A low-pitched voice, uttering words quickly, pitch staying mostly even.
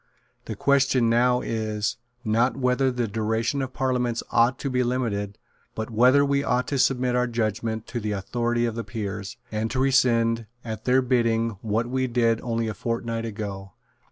No: low, 115 Hz; average, 175 wpm; narrow, 2.3 semitones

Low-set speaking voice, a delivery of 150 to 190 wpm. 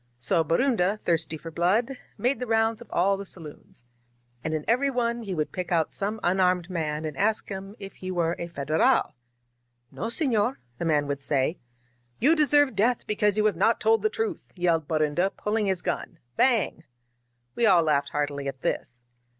No: medium, 185 Hz; average, 185 wpm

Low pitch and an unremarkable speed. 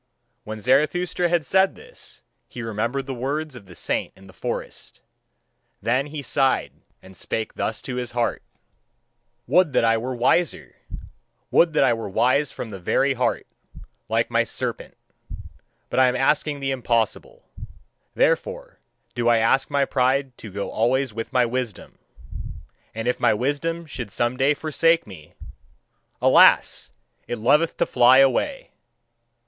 Yes: low, 130 Hz; average, 150 wpm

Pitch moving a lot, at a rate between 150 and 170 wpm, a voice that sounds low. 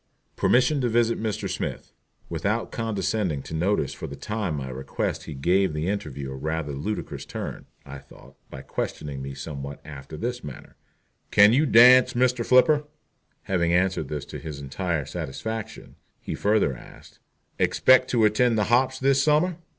Yes: wide, 8.4 semitones; average, 160 wpm; low, 100 Hz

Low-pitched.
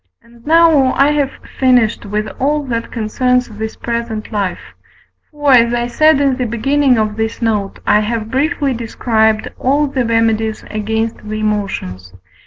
No: high, 235 Hz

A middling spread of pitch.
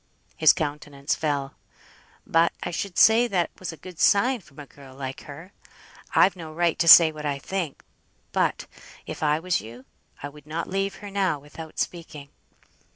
Yes: average, 4.0 semitones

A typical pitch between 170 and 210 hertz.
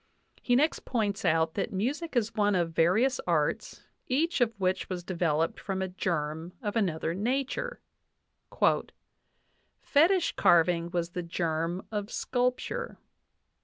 Yes: high, 190 Hz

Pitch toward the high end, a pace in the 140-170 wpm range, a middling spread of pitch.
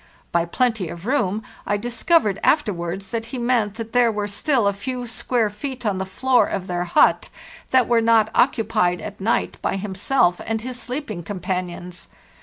No: high, 220 Hz; average, 180 wpm; average, 4.3 semitones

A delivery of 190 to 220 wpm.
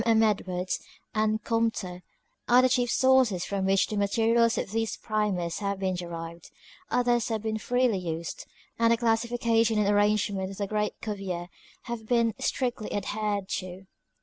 No: average, 155 wpm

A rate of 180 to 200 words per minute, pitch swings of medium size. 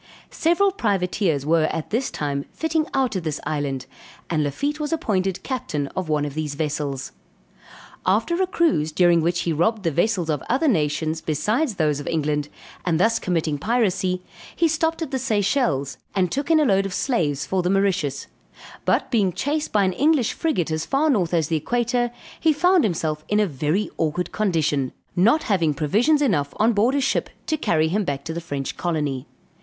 No: average, 190 wpm; wide, 8.0 semitones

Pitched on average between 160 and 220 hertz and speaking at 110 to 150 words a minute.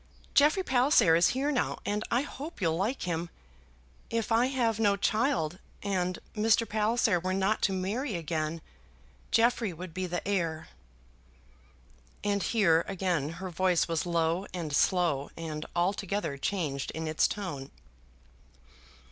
Yes: medium, 185 Hz; average, 140 wpm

